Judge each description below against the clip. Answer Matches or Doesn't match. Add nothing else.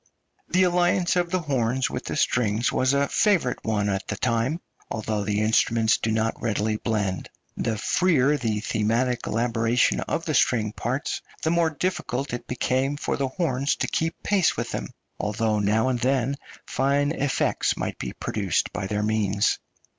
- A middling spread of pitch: Matches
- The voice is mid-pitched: Doesn't match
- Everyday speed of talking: Matches